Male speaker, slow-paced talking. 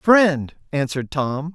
Yes: male; slow, 115 wpm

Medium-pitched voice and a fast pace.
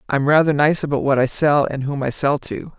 Yes: medium, 145 Hz; fast, 260 wpm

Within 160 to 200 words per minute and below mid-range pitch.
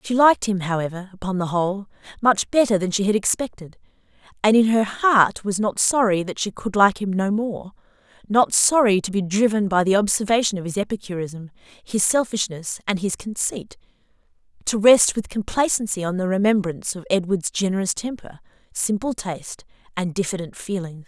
No: average, 165 wpm; high, 200 Hz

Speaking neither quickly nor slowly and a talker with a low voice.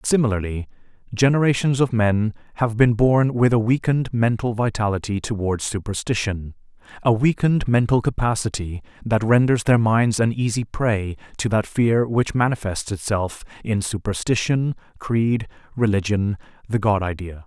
No: slow, 125 wpm; low, 110 Hz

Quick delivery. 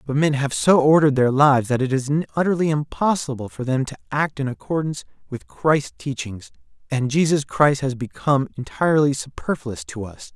No: average, 175 wpm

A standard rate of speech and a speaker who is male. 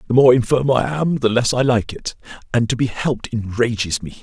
No: fast, 215 wpm; male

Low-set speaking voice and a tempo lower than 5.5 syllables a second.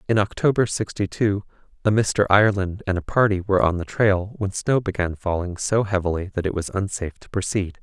No: low, 100 Hz; 5.6 syllables/s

